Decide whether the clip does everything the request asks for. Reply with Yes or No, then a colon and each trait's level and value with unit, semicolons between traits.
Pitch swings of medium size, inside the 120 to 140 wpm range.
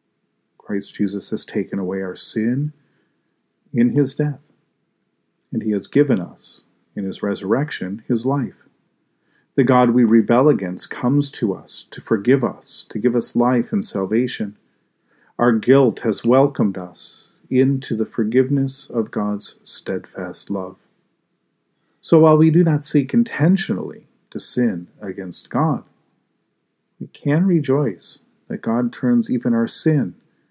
Yes: average, 4.6 semitones; slow, 135 wpm